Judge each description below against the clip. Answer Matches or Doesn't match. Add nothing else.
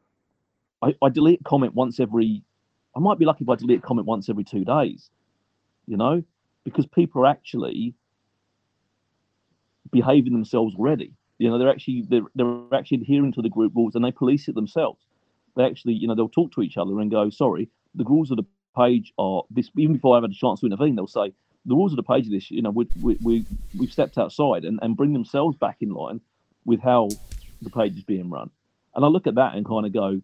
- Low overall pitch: Matches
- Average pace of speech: Doesn't match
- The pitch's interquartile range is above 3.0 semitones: Matches